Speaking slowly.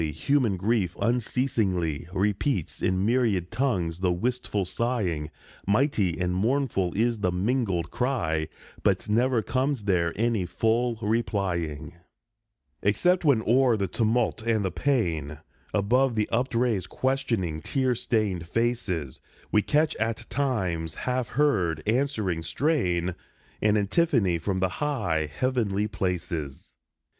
Yes: slow, 120 wpm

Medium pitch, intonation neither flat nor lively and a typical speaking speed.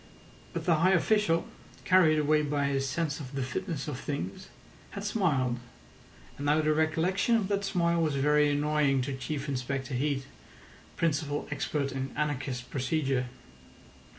Yes: medium, 150 Hz; average, 3.3 semitones; average, 150 wpm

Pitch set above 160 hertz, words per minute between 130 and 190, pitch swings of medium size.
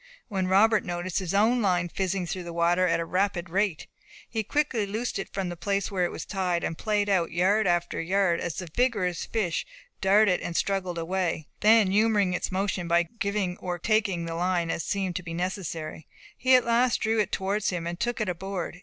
No: high, 190 Hz; fast, 205 wpm; average, 3.0 semitones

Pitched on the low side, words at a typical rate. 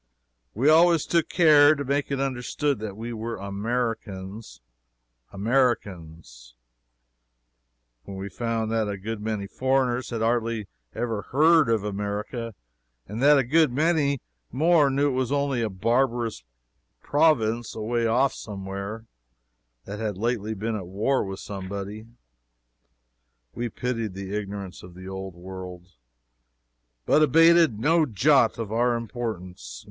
No: low, 115 Hz; slow, 130 wpm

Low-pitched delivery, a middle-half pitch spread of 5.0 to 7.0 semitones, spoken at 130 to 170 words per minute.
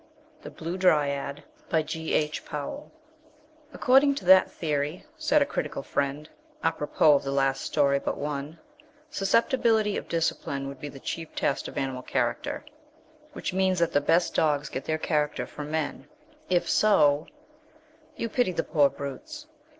No: medium, 155 Hz; average, 5.3 semitones; average, 150 wpm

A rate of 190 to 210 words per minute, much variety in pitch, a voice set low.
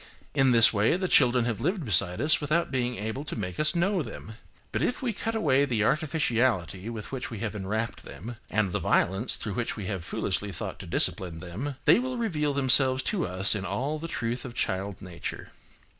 Yes: fast, 205 wpm; wide, 6.4 semitones; low, 120 Hz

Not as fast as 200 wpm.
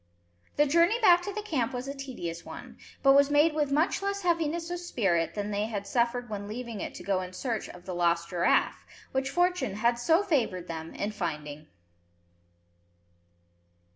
Yes: average, 180 wpm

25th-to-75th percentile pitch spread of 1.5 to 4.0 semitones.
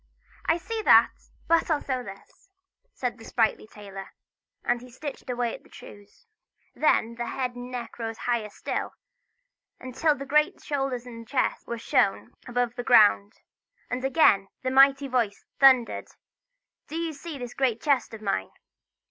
Yes: average, 3.3 semitones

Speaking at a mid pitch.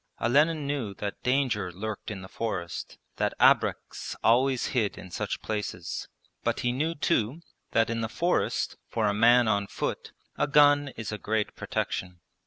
No: low, 115 Hz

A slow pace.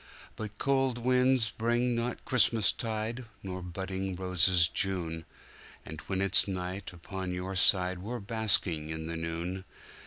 Yes: slow, 125 wpm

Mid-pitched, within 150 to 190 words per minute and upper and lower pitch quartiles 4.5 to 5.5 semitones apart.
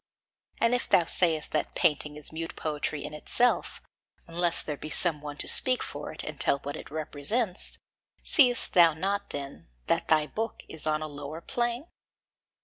Yes: medium, 160 Hz; average, 175 wpm; average, 5.1 semitones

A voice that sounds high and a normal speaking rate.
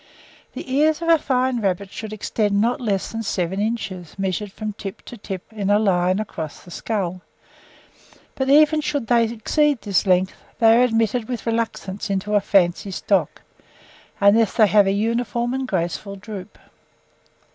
Yes: high, 210 Hz; average, 165 wpm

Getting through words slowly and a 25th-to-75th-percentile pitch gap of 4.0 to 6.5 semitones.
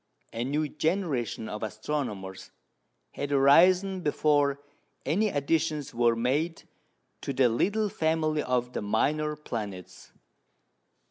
Yes: slow, 110 wpm; average, 4.9 semitones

